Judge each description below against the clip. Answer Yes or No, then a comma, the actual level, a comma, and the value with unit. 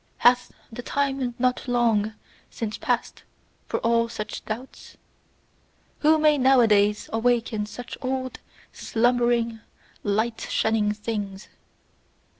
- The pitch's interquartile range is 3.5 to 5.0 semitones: No, narrow, 2.5 semitones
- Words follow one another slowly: Yes, slow, 100 wpm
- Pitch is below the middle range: No, high, 235 Hz